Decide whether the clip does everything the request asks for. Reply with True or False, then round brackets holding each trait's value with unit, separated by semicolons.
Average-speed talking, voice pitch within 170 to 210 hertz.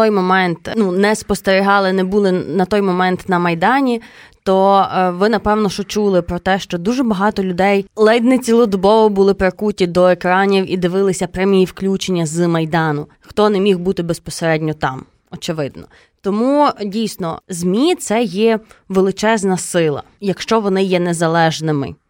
True (145 wpm; 190 Hz)